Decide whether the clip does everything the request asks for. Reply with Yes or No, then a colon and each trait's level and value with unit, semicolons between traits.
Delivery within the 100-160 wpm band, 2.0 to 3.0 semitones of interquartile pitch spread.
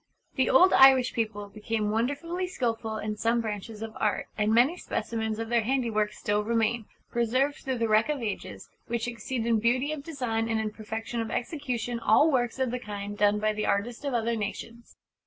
No: average, 195 wpm; average, 2.7 semitones